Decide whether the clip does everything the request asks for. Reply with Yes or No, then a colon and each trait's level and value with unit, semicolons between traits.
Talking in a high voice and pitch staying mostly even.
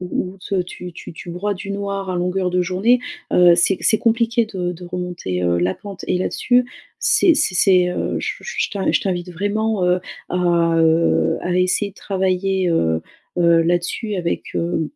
No: medium, 180 Hz; narrow, 2.2 semitones